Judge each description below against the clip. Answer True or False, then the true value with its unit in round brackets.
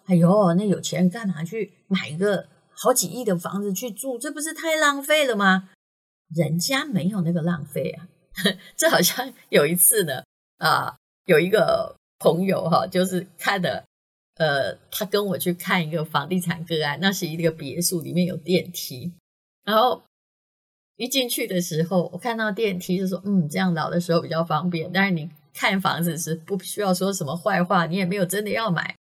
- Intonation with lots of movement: False (3.1 semitones)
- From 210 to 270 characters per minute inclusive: True (265 characters per minute)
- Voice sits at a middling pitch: True (180 Hz)